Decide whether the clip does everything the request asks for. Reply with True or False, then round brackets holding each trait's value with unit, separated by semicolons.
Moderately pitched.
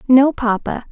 False (250 Hz)